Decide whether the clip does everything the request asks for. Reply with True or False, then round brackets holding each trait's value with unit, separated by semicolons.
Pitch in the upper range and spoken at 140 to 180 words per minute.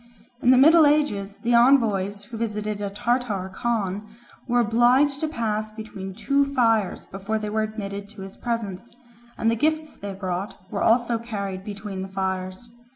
True (215 Hz; 165 wpm)